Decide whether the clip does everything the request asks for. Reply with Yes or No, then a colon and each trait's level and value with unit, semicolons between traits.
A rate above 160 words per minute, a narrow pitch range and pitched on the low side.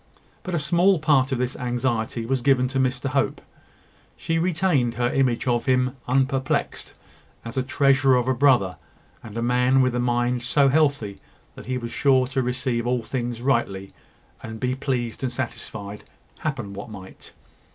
Yes: average, 170 wpm; narrow, 2.2 semitones; low, 125 Hz